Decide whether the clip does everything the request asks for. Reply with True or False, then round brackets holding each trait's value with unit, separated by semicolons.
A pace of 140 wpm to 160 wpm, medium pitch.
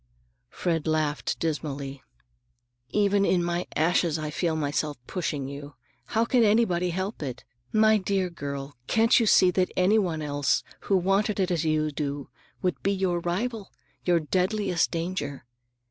True (145 wpm; 175 Hz)